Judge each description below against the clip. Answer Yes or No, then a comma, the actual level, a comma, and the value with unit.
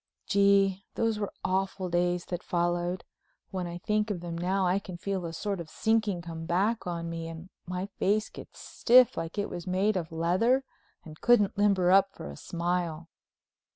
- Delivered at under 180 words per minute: No, average, 185 wpm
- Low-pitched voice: No, medium, 185 Hz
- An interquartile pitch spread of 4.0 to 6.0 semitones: No, average, 2.7 semitones